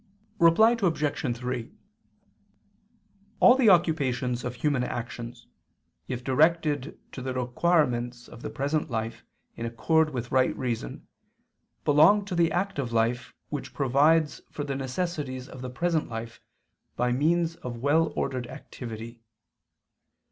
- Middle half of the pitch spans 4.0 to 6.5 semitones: Yes, average, 4.7 semitones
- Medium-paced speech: No, slow, 125 wpm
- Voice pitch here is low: Yes, low, 130 Hz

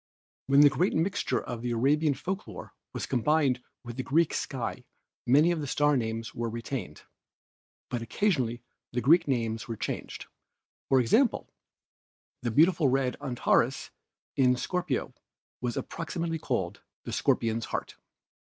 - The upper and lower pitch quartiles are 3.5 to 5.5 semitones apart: Yes, average, 5.0 semitones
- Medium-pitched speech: No, low, 130 Hz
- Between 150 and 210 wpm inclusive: No, average, 140 wpm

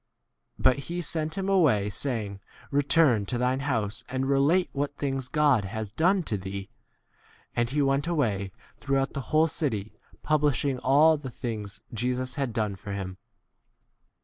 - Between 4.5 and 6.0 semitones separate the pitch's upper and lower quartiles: Yes, average, 5.3 semitones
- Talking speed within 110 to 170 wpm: Yes, average, 165 wpm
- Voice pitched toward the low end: Yes, low, 130 Hz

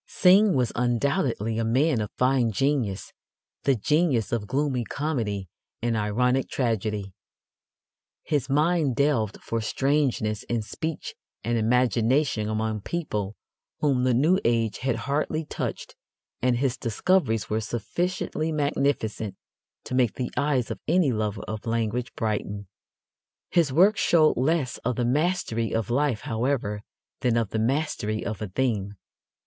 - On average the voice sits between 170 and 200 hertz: No, low, 125 Hz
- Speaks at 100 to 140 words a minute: Yes, slow, 135 wpm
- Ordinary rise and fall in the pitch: Yes, average, 4.6 semitones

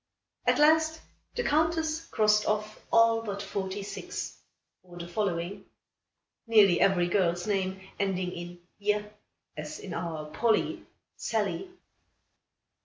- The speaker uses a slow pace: Yes, slow, 115 wpm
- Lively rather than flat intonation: No, average, 4.3 semitones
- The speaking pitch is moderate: No, high, 200 Hz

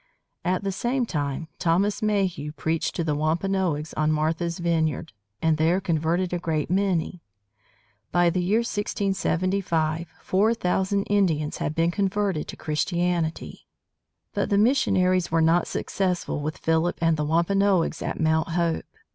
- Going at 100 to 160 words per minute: Yes, average, 140 wpm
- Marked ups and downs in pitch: No, average, 3.3 semitones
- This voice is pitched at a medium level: Yes, medium, 170 Hz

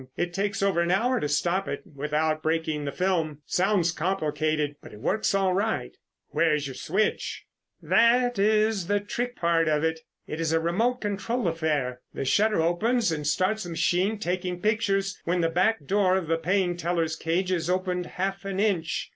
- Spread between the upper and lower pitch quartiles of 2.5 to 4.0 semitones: Yes, average, 3.7 semitones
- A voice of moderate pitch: Yes, medium, 180 Hz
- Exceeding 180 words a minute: Yes, average, 190 wpm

